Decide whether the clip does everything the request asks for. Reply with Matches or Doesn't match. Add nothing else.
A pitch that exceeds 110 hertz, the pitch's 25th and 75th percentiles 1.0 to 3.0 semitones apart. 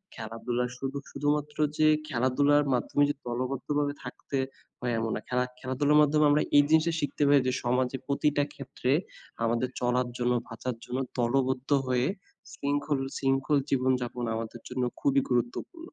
Matches